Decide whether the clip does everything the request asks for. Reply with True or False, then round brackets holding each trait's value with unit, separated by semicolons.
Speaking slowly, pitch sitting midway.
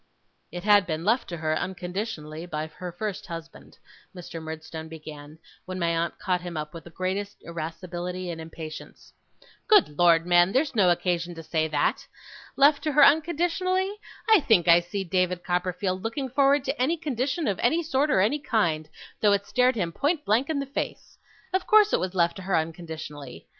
False (185 wpm; 180 Hz)